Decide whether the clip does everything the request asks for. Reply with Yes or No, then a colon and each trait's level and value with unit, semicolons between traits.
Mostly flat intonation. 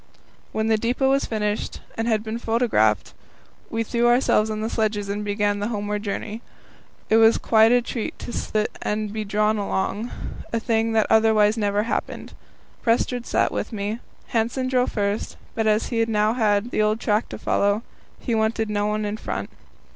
Yes: narrow, 1.5 semitones